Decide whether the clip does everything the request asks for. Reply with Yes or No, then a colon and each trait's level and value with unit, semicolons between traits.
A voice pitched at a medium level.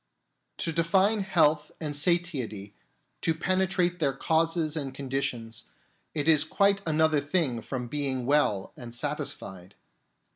Yes: medium, 150 Hz